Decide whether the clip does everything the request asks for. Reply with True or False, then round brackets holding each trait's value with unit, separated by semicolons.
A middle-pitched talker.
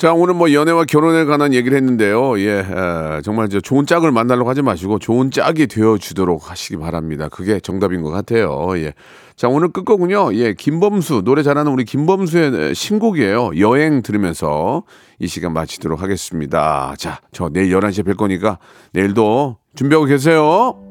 False (115 Hz)